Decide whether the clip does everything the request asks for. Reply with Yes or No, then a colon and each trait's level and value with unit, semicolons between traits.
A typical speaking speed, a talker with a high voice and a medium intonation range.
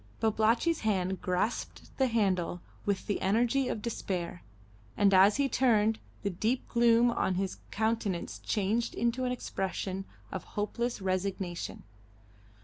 No: slow, 130 wpm; high, 210 Hz; average, 3.7 semitones